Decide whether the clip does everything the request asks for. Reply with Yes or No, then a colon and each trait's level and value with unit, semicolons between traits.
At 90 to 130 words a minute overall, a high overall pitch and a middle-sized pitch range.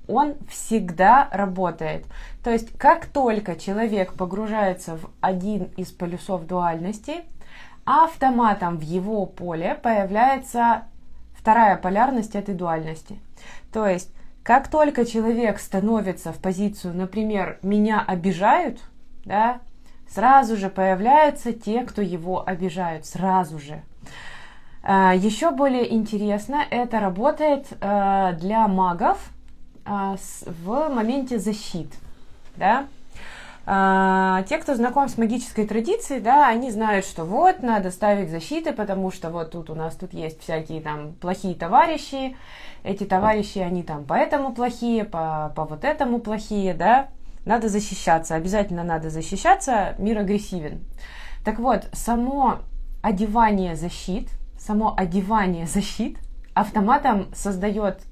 Yes: average, 115 wpm; high, 205 Hz; average, 4.2 semitones